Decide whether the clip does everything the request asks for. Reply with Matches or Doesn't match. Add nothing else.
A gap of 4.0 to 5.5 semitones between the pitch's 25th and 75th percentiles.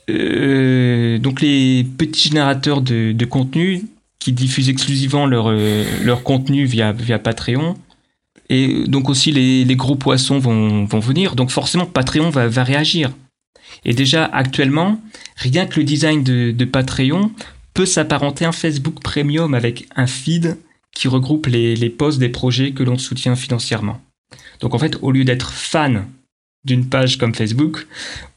Doesn't match